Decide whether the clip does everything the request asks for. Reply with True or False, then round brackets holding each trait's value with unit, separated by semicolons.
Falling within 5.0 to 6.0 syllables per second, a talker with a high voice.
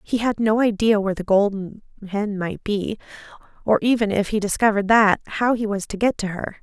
True (5.6 syllables/s; 210 Hz)